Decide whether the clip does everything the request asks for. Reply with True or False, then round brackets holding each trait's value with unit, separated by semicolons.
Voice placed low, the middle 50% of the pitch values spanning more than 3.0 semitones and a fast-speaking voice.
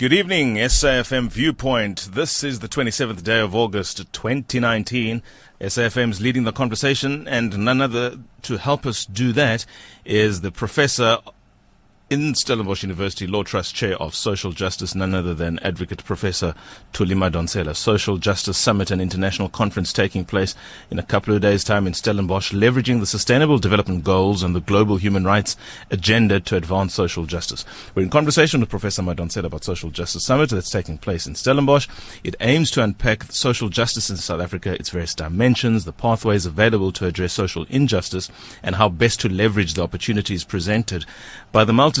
False (105 Hz; 3.8 semitones; 170 wpm)